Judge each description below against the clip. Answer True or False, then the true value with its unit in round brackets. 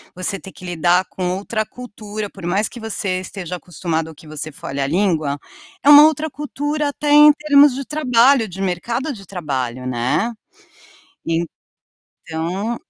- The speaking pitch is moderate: False (195 Hz)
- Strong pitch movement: True (7.6 semitones)